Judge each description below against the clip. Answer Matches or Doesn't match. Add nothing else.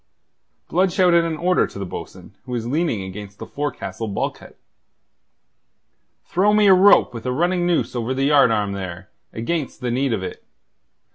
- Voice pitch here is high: Doesn't match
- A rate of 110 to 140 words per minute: Doesn't match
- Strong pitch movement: Matches